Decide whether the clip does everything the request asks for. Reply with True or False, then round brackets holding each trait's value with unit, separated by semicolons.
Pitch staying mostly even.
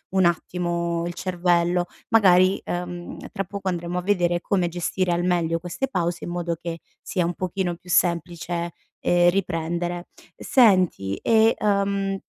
True (1.4 semitones)